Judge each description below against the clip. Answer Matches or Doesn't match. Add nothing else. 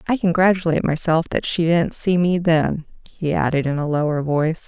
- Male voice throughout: Doesn't match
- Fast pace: Doesn't match